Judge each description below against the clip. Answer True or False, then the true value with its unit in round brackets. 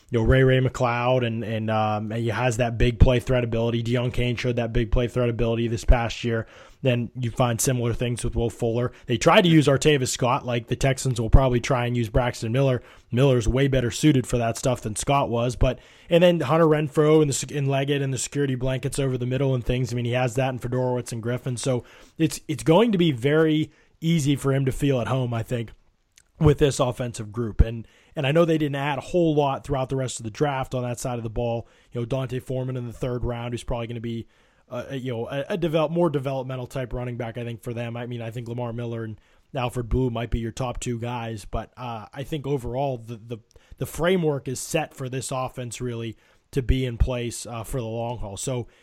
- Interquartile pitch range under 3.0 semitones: True (2.5 semitones)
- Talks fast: True (245 wpm)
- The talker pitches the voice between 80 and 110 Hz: False (125 Hz)